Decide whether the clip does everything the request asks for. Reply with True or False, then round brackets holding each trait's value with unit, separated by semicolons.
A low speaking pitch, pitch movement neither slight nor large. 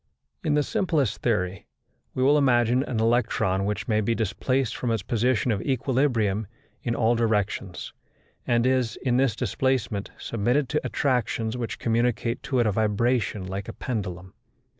True (115 Hz; 3.4 semitones)